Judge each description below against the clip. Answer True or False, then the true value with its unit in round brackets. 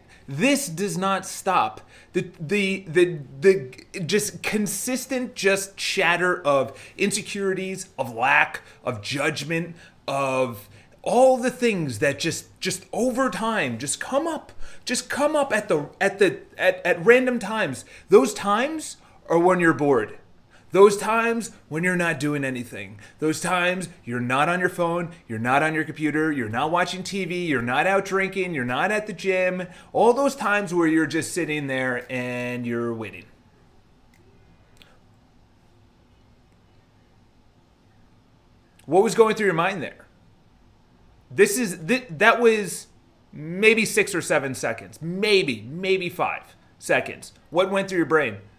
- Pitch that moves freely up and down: True (6.6 semitones)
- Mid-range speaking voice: True (180 Hz)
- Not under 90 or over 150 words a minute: True (145 wpm)